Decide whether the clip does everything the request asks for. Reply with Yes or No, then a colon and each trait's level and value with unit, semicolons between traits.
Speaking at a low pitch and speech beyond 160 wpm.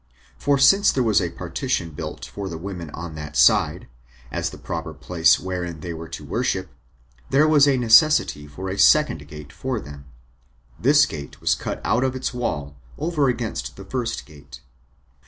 Yes: very low, 95 Hz; average, 175 wpm